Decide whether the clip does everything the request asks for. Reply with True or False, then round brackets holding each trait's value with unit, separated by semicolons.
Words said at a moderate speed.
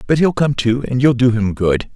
False (275 wpm)